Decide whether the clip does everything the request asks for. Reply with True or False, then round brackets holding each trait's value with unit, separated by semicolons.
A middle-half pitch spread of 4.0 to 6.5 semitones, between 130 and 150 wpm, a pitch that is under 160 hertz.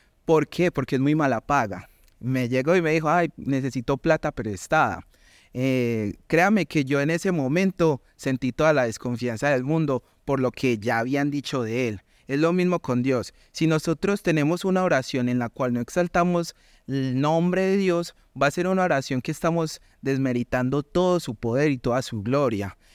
False (4.8 semitones; 185 wpm; 140 Hz)